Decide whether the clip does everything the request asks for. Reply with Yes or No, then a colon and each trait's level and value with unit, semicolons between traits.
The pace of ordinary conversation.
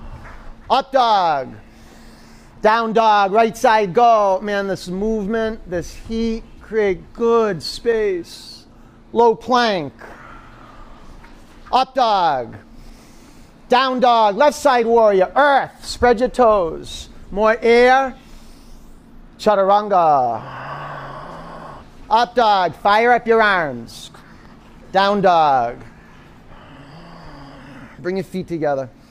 No: slow, 90 wpm